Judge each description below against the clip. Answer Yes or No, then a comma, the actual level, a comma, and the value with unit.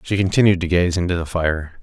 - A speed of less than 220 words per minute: No, fast, 230 wpm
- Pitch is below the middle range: Yes, very low, 90 Hz